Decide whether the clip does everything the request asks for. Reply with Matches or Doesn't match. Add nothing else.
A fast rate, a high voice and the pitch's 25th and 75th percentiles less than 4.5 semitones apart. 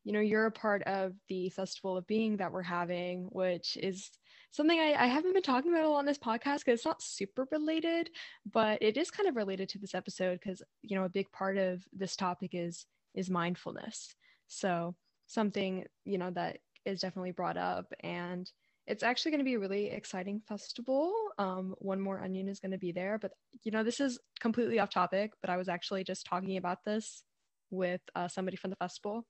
Matches